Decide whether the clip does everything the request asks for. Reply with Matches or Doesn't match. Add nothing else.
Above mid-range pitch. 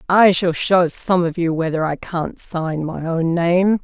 Doesn't match